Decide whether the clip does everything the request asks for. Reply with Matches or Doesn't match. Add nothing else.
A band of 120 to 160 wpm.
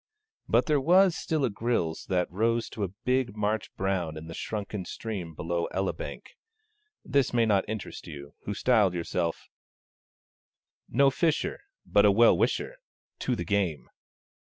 Matches